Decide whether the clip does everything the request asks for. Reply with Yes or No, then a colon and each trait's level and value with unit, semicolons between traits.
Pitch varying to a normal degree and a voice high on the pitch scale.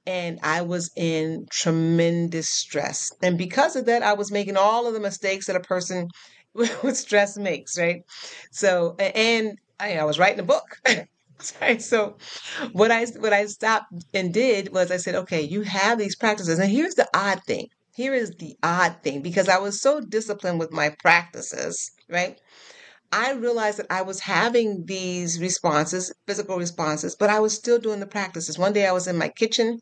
Yes: average, 3.9 semitones; high, 195 Hz